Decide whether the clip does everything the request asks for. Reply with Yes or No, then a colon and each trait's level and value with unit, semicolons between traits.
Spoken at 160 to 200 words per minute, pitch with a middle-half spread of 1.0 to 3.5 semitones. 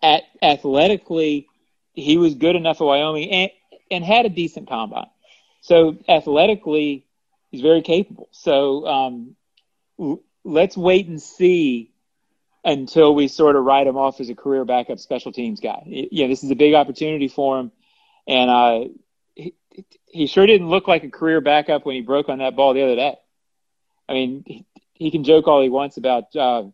No: average, 175 wpm; average, 4.8 semitones